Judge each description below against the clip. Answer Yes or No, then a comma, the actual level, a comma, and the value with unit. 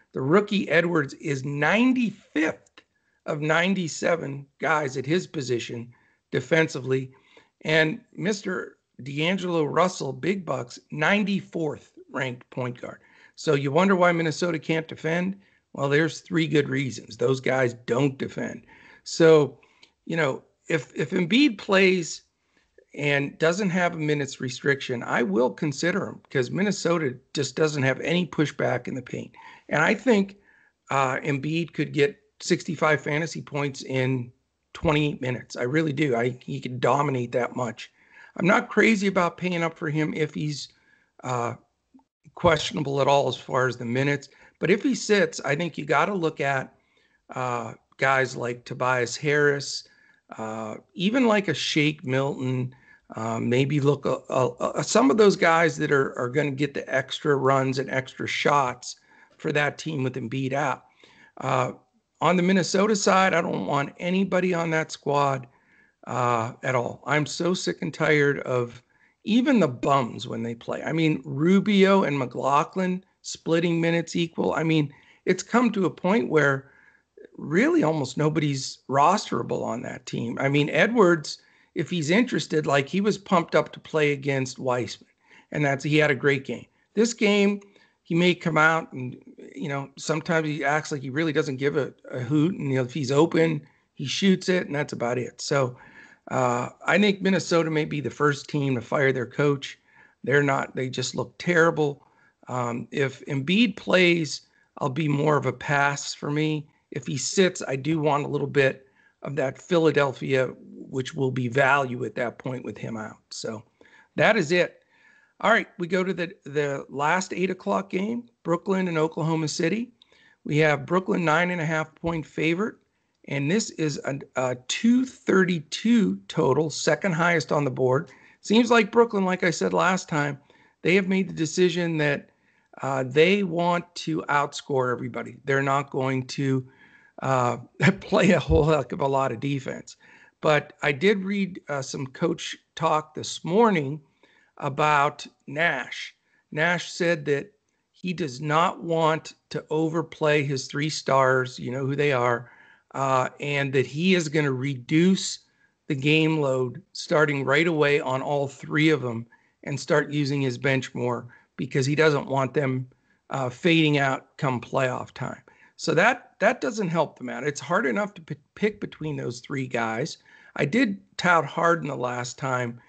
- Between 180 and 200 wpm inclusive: No, average, 165 wpm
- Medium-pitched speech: Yes, medium, 150 Hz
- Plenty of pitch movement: No, average, 4.3 semitones